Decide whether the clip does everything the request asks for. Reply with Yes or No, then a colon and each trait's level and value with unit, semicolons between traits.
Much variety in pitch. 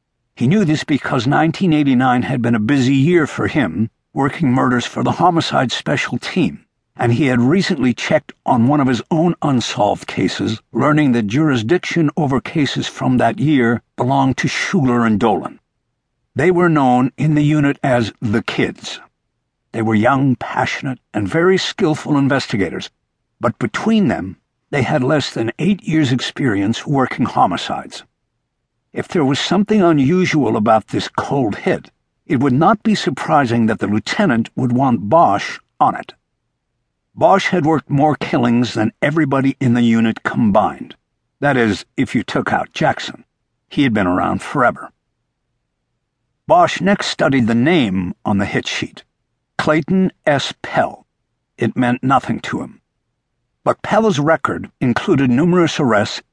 No: average, 4.7 semitones